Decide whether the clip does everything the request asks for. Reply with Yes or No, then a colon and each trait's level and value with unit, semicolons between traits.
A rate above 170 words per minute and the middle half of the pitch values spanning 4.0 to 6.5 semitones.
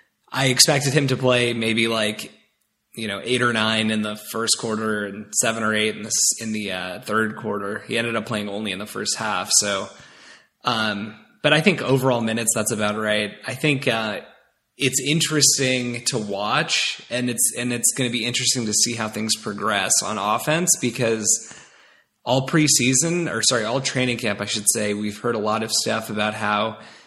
No: average, 195 wpm; average, 3.1 semitones